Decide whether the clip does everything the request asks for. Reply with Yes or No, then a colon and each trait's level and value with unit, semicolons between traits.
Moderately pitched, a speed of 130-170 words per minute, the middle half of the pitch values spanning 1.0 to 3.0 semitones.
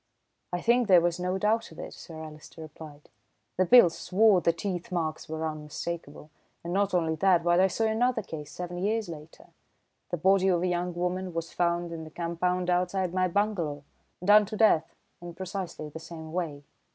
No: medium, 175 Hz; average, 190 wpm; average, 2.7 semitones